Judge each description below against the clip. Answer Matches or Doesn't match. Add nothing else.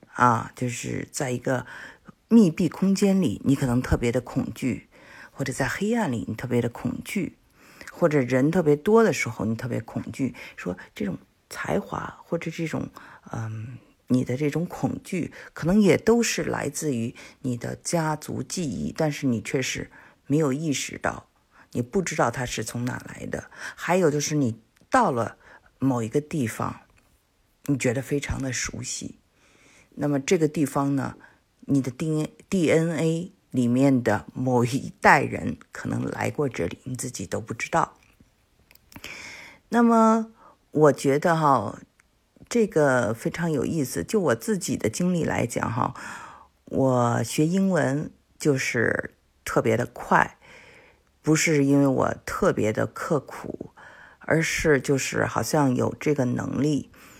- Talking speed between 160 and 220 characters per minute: Matches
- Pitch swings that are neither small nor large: Matches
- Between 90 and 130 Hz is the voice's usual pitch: Doesn't match